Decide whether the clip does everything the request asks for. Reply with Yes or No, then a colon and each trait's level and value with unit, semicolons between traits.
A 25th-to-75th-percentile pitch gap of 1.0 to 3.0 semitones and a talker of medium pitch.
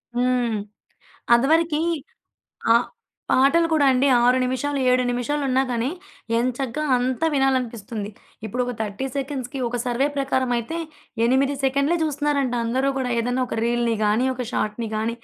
No: narrow, 2.6 semitones; very high, 255 Hz